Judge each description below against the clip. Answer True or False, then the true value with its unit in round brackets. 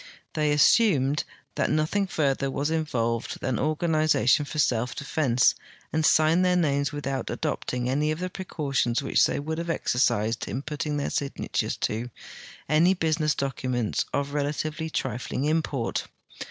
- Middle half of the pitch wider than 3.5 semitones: False (3.1 semitones)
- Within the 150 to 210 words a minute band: False (140 wpm)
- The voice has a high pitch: False (145 Hz)